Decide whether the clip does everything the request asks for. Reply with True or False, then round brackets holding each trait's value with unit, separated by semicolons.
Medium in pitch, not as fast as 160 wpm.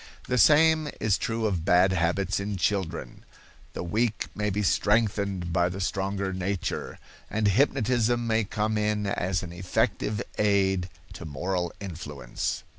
False (100 Hz; 140 wpm)